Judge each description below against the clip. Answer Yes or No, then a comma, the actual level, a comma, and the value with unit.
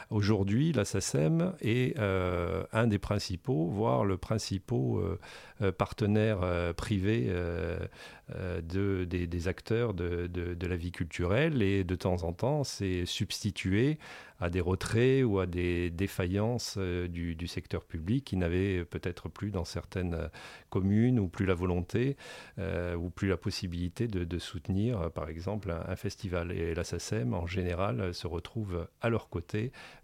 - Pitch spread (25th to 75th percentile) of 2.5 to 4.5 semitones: Yes, average, 3.5 semitones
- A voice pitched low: Yes, very low, 95 Hz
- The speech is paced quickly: No, average, 155 wpm